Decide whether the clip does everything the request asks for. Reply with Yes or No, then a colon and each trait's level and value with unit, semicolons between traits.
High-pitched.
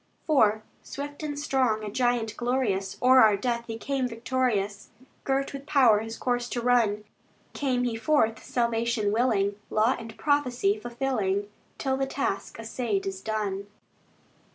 Yes: high, 235 Hz